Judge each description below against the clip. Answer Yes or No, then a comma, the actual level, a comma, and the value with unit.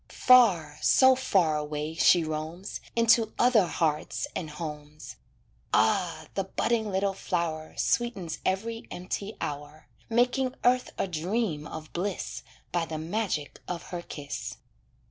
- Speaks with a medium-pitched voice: Yes, medium, 175 Hz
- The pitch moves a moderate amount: No, wide, 6.1 semitones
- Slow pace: Yes, slow, 125 wpm